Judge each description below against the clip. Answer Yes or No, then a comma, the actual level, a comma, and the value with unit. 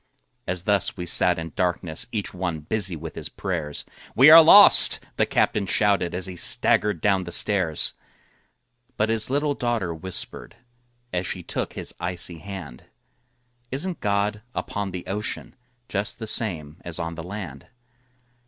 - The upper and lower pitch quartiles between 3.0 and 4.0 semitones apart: Yes, average, 3.6 semitones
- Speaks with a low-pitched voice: Yes, very low, 95 Hz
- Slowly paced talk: No, average, 155 wpm